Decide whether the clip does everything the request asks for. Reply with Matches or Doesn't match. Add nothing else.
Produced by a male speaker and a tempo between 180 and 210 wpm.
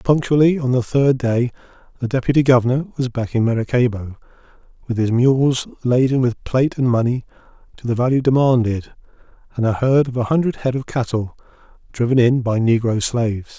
Doesn't match